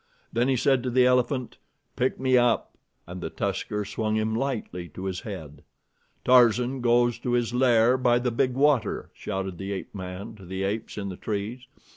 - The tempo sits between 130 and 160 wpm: No, average, 185 wpm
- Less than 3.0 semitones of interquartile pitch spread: No, average, 4.1 semitones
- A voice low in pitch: Yes, low, 115 Hz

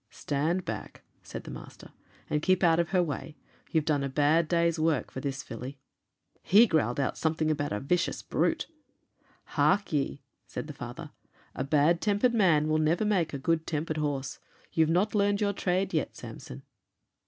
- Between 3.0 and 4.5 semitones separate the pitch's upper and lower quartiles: Yes, average, 3.7 semitones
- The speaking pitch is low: No, medium, 160 Hz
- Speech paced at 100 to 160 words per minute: No, average, 175 wpm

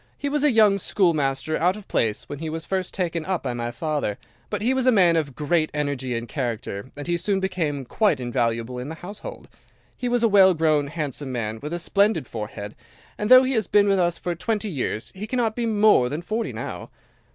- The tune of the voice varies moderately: No, wide, 7.3 semitones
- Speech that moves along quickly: Yes, fast, 220 wpm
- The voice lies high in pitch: No, medium, 165 Hz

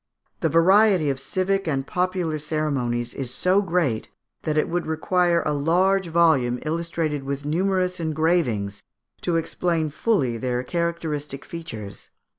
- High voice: No, medium, 160 Hz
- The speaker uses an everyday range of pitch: Yes, average, 4.3 semitones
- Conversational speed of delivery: No, slow, 130 wpm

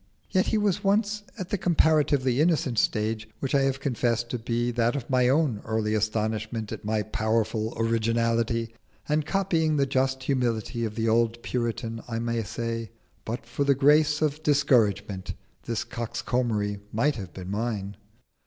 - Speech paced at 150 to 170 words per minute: Yes, average, 160 wpm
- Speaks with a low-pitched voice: Yes, low, 120 Hz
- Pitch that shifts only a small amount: No, average, 4.2 semitones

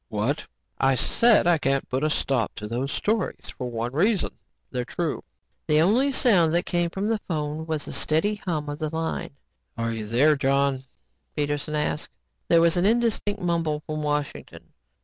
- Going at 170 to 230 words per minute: Yes, average, 175 wpm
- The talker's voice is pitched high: No, medium, 155 Hz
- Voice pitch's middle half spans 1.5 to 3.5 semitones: No, average, 4.2 semitones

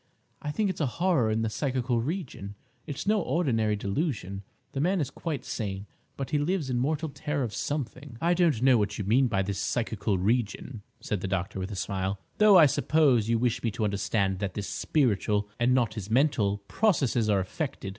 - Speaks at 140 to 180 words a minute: No, average, 200 wpm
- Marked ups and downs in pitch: Yes, wide, 6.3 semitones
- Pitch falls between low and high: No, low, 120 Hz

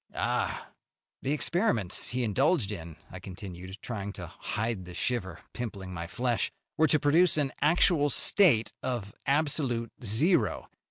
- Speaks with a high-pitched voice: No, low, 120 Hz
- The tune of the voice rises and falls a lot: Yes, wide, 7.1 semitones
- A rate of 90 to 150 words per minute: Yes, average, 140 wpm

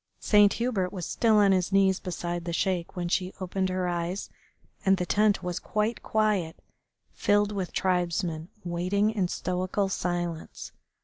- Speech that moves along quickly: No, average, 150 wpm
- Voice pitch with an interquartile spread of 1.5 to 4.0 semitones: Yes, narrow, 2.5 semitones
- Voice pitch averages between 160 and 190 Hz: Yes, medium, 185 Hz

